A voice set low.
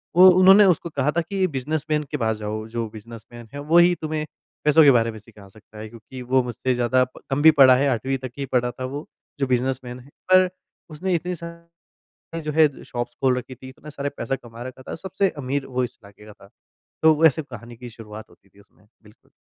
Yes: low, 130 Hz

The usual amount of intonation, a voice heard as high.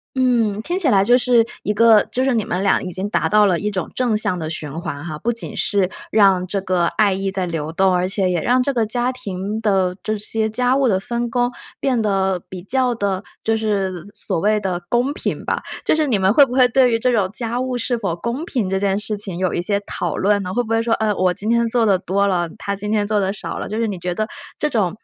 Yes: average, 3.9 semitones; high, 210 Hz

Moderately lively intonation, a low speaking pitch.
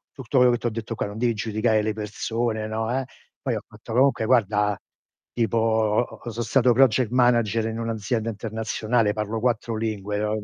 No: narrow, 1.8 semitones; low, 110 Hz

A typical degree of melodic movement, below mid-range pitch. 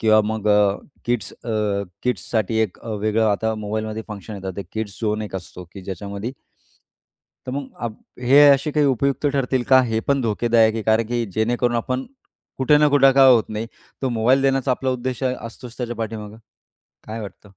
Yes: average, 3.2 semitones; low, 115 Hz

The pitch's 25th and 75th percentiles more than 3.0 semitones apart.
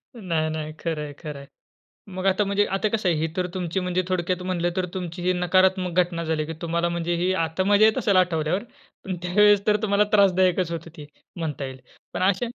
No: narrow, 2.5 semitones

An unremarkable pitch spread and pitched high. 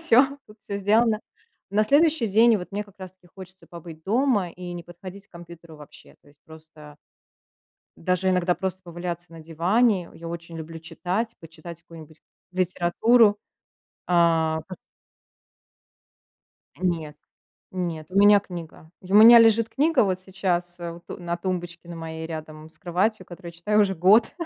No: average, 3.5 semitones; medium, 180 Hz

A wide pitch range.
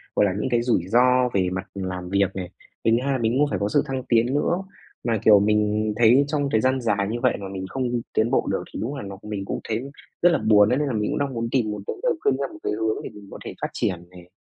No: average, 4.3 semitones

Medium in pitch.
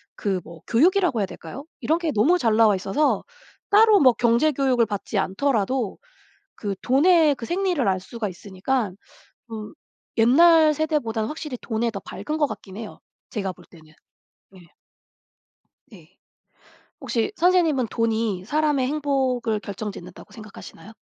No: high, 235 Hz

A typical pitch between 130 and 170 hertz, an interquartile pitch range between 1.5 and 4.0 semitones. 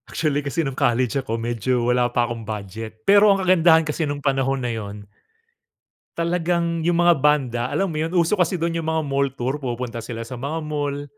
No: medium, 140 Hz; average, 5.2 semitones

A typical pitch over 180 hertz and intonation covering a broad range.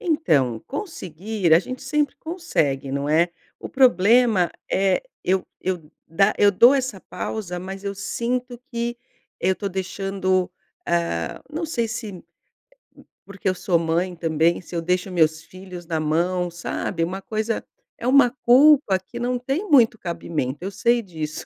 Yes: high, 190 Hz; wide, 6.0 semitones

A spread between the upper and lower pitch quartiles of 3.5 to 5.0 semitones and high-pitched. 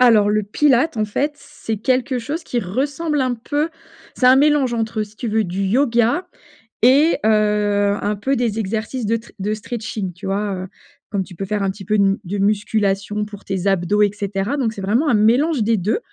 Yes: average, 3.8 semitones; high, 215 Hz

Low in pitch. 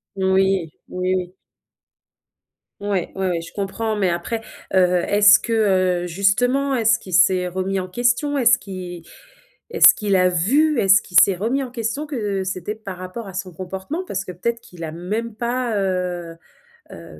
No: high, 195 Hz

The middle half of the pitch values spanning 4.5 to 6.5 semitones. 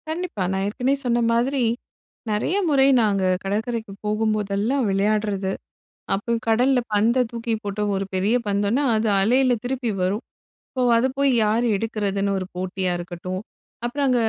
No: average, 3.7 semitones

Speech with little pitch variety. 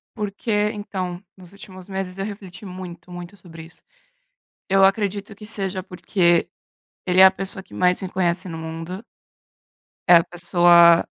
Yes: narrow, 1.9 semitones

